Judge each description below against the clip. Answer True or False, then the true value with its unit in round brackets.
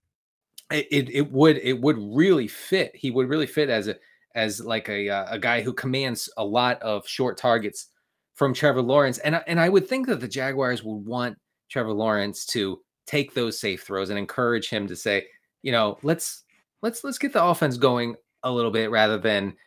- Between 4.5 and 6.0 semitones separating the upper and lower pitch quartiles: True (4.8 semitones)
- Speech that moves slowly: False (200 wpm)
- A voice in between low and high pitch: False (125 Hz)